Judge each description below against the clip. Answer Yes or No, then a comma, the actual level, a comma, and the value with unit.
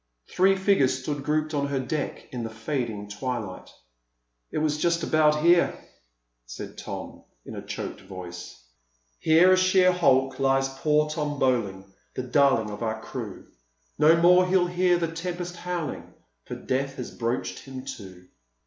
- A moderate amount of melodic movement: No, wide, 5.8 semitones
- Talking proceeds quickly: No, average, 155 wpm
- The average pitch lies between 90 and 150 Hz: Yes, medium, 140 Hz